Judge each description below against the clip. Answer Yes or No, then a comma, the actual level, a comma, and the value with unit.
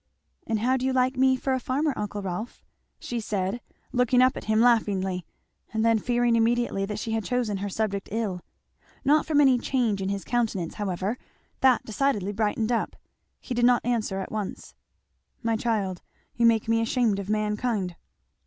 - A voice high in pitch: Yes, high, 225 Hz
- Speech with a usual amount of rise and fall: Yes, average, 3.3 semitones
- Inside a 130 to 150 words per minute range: No, average, 180 wpm